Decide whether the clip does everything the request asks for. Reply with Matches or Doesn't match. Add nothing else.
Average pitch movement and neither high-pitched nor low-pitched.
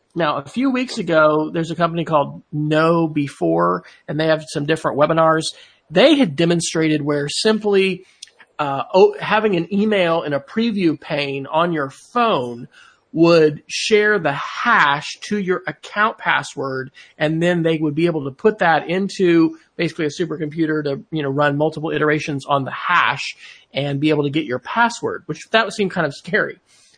Matches